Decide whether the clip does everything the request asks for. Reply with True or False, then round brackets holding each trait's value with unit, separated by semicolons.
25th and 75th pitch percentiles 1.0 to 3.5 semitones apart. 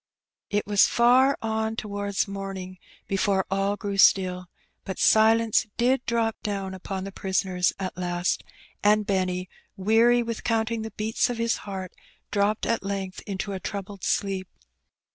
True (2.6 semitones)